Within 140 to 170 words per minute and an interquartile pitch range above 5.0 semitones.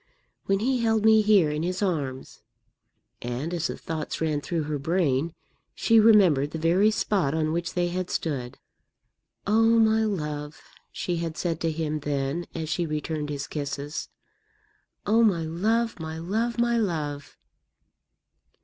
Yes: average, 150 wpm; wide, 5.5 semitones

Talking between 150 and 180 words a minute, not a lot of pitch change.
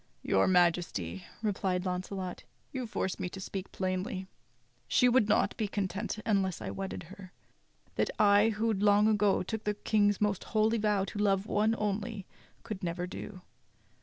Yes: average, 160 wpm; narrow, 2.2 semitones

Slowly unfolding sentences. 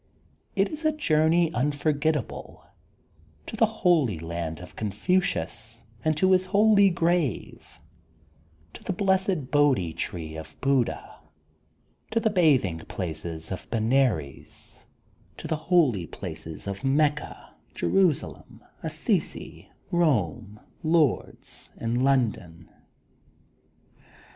Yes: slow, 105 wpm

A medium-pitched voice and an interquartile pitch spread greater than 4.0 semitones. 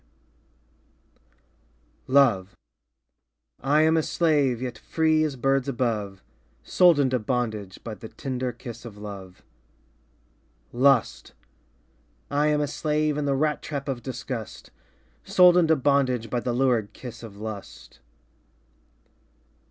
No: low, 130 Hz; average, 4.4 semitones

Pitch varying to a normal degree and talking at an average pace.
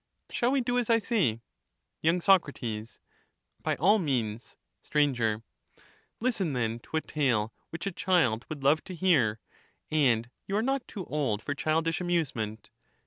No: wide, 8.0 semitones; average, 150 wpm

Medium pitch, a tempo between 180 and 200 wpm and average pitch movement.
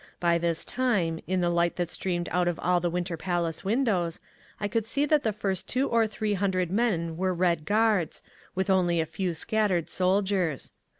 Yes: medium, 180 Hz; average, 190 wpm; average, 3.2 semitones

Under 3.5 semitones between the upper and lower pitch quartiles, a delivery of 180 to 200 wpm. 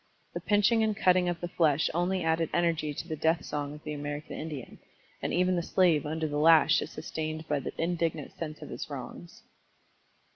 Yes: narrow, 2.5 semitones; average, 195 wpm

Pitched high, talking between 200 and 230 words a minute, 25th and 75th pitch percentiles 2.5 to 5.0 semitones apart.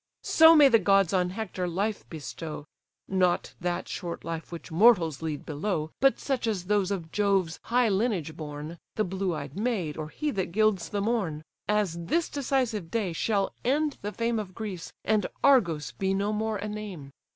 No: high, 195 Hz; average, 180 wpm; average, 4.7 semitones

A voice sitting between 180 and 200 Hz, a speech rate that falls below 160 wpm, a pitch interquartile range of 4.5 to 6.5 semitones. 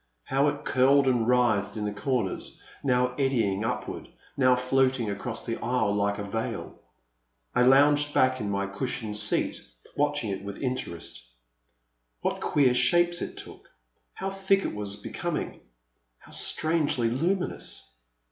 No: low, 125 Hz; average, 145 wpm; average, 5.1 semitones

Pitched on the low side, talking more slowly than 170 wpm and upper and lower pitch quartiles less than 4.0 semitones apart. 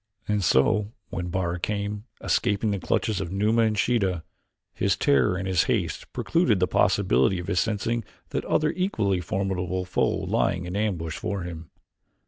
Yes: very low, 95 Hz; average, 160 wpm; average, 3.1 semitones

